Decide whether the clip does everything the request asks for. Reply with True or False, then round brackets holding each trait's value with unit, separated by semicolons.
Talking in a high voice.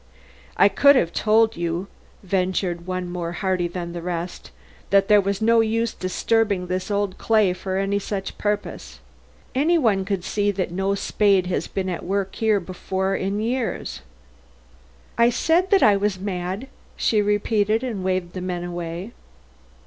True (195 Hz)